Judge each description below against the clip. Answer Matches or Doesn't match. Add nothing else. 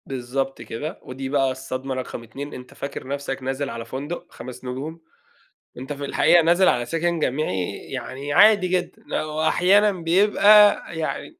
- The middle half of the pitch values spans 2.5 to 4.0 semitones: Doesn't match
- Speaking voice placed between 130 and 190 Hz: Matches